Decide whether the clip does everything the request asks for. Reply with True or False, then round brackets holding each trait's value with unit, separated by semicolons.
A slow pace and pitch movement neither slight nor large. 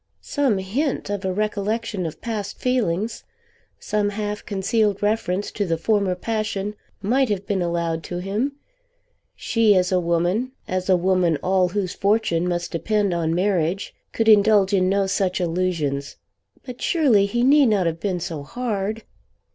False (155 wpm; 3.2 semitones)